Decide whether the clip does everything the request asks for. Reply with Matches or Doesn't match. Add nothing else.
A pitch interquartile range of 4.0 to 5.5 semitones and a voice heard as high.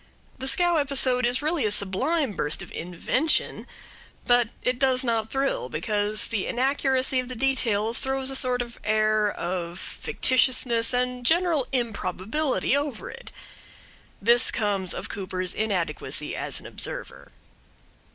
Matches